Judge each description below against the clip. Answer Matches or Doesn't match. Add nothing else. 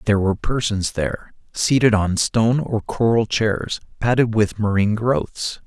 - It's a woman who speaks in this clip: Doesn't match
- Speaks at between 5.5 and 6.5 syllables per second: Doesn't match